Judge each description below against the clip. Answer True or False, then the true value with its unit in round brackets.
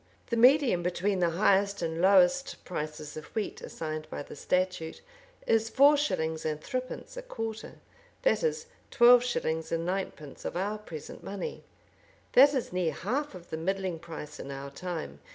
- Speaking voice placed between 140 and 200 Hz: True (185 Hz)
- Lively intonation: True (6.3 semitones)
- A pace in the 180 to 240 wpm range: False (165 wpm)